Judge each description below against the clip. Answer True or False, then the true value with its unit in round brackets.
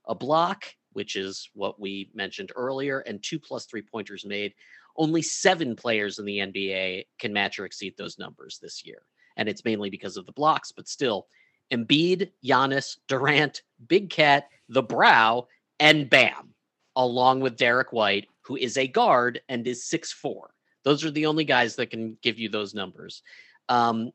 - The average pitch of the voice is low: True (125 Hz)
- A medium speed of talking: True (175 wpm)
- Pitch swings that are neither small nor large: True (4.6 semitones)